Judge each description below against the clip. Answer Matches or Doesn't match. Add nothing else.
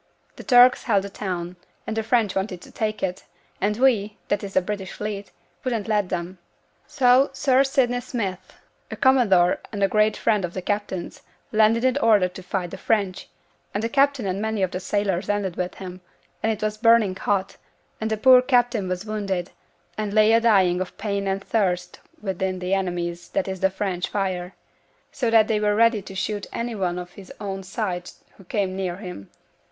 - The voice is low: Doesn't match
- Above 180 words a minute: Matches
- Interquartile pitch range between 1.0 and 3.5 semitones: Matches